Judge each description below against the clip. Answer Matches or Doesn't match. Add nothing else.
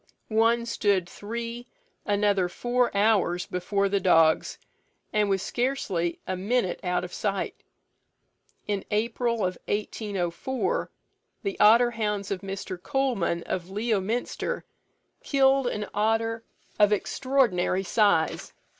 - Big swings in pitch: Doesn't match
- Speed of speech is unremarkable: Doesn't match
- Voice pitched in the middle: Doesn't match